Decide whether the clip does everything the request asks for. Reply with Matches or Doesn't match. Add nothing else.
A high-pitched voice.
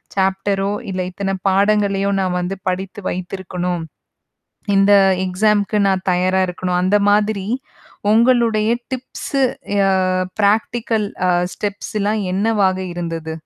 Matches